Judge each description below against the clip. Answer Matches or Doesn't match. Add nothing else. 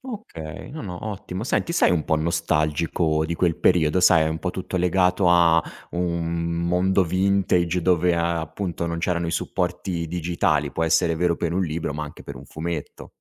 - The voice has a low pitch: Matches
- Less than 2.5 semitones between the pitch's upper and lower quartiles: Matches